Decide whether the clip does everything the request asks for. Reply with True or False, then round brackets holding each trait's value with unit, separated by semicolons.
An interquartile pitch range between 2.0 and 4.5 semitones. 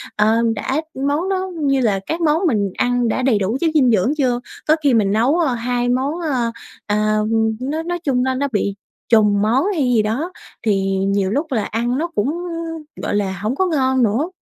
False (5.3 semitones)